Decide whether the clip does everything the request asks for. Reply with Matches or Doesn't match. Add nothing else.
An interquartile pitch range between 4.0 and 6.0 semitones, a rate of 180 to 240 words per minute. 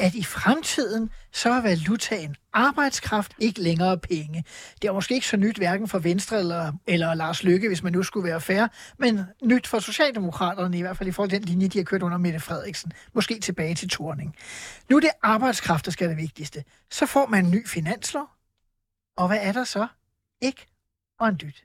Matches